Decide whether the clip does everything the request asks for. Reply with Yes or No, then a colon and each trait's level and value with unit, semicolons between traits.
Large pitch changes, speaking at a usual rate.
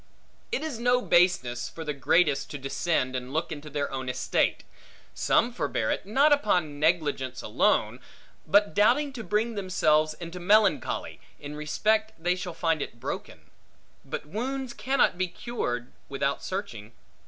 Yes: wide, 7.0 semitones; average, 150 wpm